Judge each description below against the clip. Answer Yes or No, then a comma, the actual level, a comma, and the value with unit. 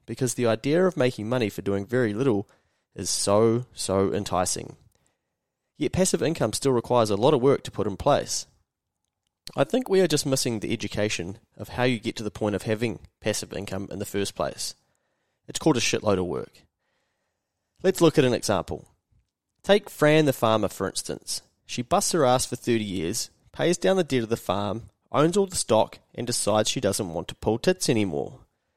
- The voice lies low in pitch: Yes, low, 115 Hz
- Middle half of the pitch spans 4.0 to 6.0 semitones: Yes, average, 4.6 semitones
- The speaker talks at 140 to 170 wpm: No, average, 195 wpm